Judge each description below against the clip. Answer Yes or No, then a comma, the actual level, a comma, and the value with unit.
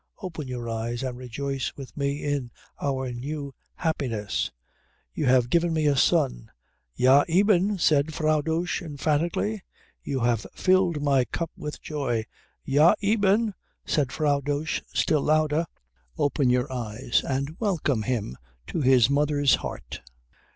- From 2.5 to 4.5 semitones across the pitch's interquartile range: Yes, average, 3.8 semitones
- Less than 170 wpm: Yes, slow, 135 wpm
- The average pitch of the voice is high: No, medium, 145 Hz